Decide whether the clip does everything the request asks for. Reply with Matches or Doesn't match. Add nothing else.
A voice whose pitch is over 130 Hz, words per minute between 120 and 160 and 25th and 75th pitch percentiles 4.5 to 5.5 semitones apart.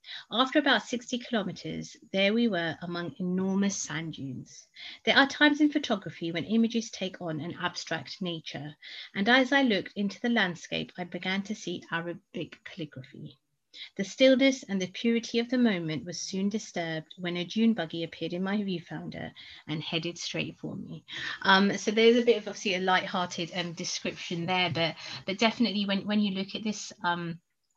Doesn't match